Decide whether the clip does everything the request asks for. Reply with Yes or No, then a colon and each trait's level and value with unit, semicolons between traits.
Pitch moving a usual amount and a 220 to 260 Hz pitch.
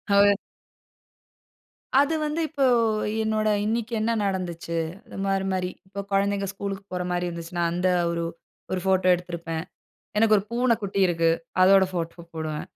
No: average, 3.4 semitones; high, 190 Hz